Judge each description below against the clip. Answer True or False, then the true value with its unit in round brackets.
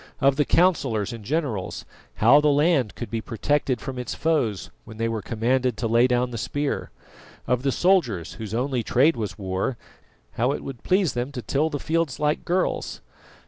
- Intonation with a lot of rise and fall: False (4.4 semitones)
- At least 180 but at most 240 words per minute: True (185 wpm)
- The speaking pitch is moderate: False (125 Hz)